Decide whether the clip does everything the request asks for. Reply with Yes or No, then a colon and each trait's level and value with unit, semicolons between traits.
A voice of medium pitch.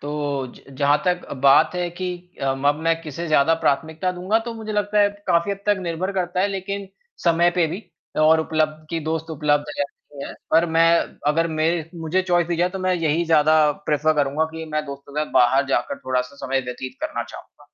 Yes: medium, 160 Hz